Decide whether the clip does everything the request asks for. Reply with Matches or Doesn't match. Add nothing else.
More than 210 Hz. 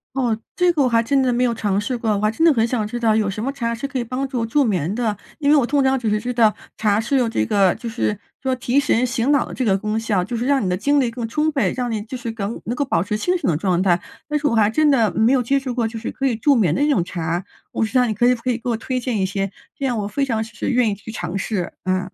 Matches